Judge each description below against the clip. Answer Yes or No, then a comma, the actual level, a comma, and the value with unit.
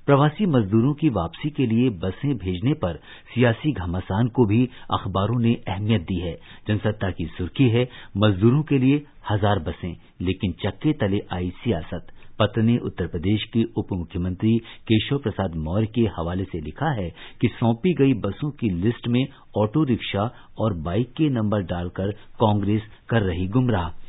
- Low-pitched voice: Yes, low, 110 Hz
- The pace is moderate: Yes, average, 160 wpm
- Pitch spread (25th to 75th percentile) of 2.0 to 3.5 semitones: No, average, 4.5 semitones